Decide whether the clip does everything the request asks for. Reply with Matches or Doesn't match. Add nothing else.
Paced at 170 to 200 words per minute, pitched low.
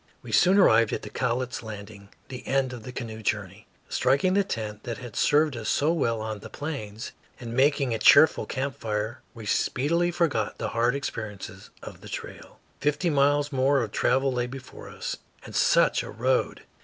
Matches